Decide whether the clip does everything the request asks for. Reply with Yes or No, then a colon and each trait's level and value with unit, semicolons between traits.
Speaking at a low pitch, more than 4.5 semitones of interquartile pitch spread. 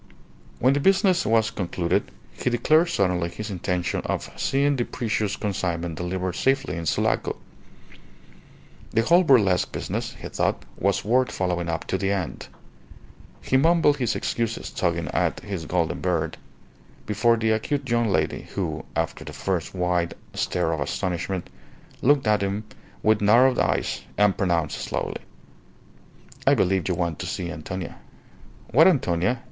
Yes: low, 100 Hz; wide, 5.5 semitones